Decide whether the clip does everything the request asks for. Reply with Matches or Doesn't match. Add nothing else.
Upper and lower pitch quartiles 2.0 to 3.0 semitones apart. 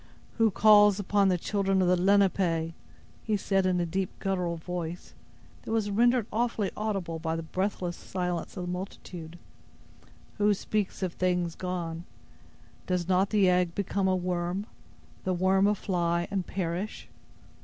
Matches